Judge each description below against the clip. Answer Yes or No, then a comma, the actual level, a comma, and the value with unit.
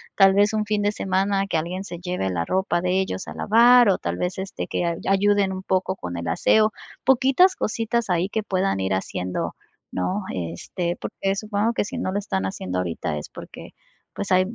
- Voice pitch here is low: No, high, 190 Hz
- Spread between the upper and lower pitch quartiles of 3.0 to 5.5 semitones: Yes, average, 3.5 semitones